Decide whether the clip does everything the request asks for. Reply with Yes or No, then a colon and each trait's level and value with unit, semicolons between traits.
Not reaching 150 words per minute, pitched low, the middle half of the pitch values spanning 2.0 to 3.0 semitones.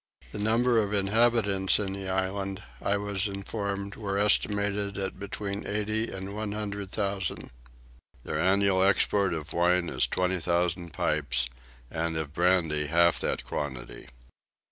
Yes: average, 140 wpm; low, 100 Hz; narrow, 2.6 semitones